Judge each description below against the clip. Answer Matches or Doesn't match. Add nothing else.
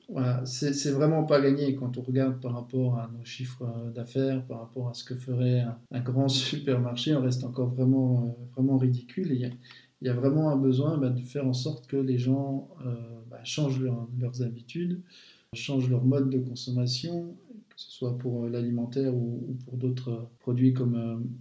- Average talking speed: Matches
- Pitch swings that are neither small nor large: Doesn't match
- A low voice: Matches